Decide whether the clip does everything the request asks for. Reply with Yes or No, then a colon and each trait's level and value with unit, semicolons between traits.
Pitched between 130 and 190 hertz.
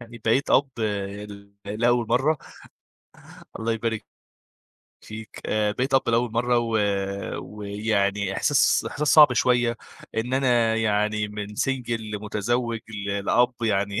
No: low, 115 Hz